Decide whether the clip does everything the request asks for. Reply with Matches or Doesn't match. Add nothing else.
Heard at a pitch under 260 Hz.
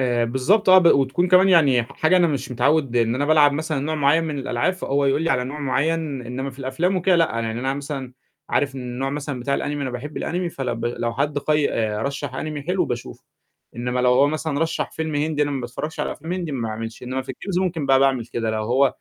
Matches